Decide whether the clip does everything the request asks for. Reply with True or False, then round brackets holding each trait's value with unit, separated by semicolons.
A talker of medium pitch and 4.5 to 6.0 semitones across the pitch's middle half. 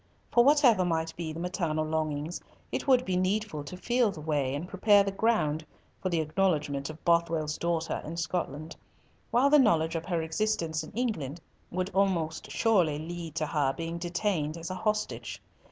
False (170 Hz; 3.8 semitones)